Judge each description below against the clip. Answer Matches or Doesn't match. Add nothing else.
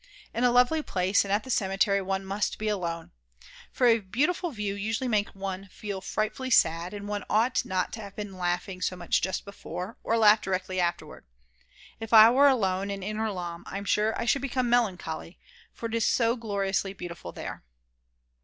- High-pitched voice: Matches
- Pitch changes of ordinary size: Matches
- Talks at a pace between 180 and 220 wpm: Matches